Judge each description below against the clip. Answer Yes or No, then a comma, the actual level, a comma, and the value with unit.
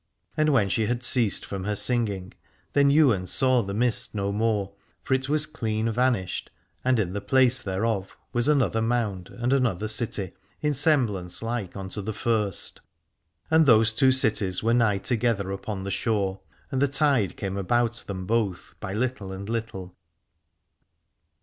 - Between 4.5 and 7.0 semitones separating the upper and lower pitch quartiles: No, average, 4.0 semitones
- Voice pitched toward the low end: Yes, low, 110 Hz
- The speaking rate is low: No, average, 160 wpm